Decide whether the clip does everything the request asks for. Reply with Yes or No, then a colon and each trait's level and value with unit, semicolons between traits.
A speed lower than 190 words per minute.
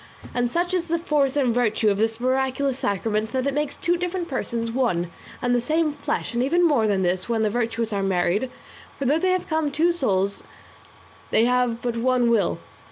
No: average, 200 wpm